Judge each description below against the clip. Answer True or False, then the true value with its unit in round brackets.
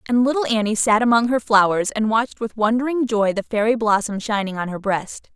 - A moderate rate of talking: False (215 wpm)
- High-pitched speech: True (220 Hz)